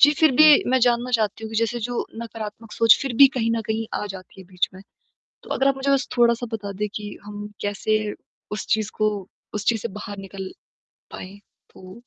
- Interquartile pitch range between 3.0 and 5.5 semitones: No, narrow, 2.6 semitones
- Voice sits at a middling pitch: No, high, 220 Hz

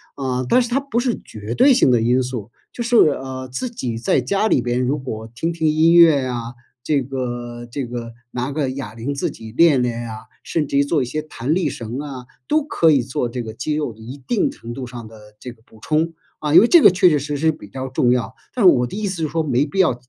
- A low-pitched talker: Yes, low, 130 Hz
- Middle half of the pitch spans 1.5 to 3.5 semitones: No, average, 4.9 semitones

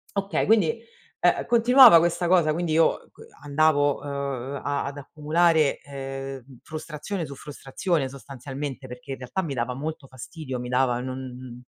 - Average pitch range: Yes, average, 3.7 semitones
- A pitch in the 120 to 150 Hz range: Yes, medium, 140 Hz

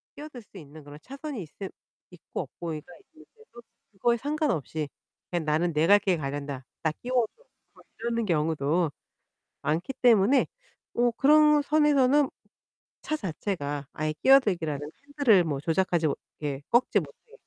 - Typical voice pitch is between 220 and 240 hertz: No, high, 190 Hz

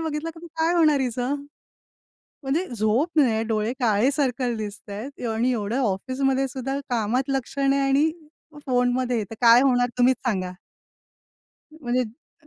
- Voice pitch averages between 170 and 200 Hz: No, very high, 255 Hz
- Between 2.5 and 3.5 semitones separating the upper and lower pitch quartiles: Yes, average, 3.2 semitones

